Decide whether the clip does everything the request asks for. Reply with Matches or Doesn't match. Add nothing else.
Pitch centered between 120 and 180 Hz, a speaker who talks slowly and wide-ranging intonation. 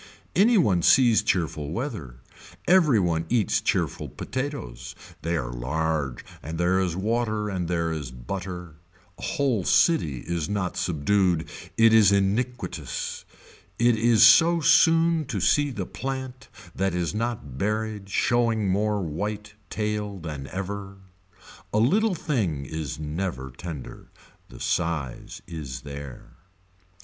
Doesn't match